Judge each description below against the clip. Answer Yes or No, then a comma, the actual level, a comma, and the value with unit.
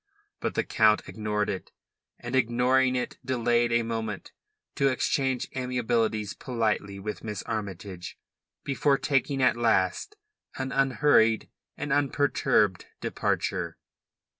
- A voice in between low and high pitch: No, low, 120 Hz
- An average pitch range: Yes, average, 3.6 semitones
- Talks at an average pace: No, slow, 115 wpm